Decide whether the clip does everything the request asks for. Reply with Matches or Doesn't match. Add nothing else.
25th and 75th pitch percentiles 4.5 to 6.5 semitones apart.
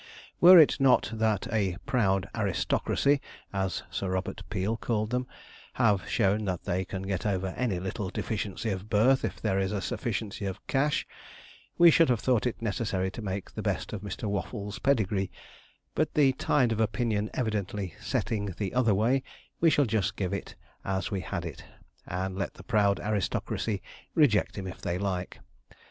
Doesn't match